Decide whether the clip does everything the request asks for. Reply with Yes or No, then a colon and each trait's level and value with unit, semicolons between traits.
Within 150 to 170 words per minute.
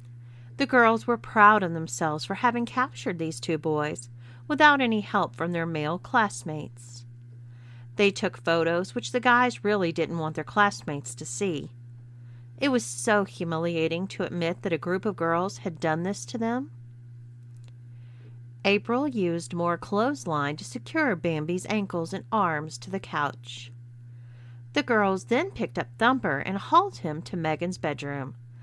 Yes: average, 155 wpm